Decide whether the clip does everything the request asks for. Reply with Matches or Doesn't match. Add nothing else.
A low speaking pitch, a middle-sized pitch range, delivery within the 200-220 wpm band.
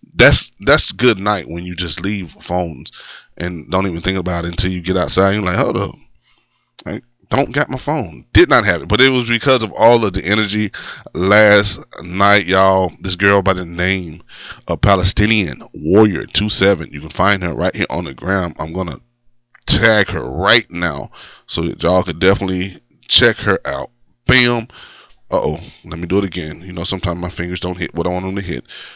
Matches